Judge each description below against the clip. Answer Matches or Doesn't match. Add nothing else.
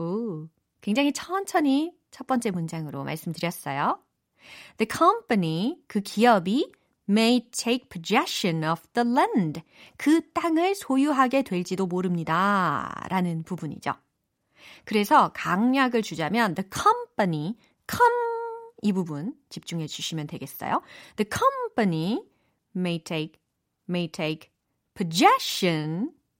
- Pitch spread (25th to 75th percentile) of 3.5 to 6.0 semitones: Doesn't match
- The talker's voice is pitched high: Matches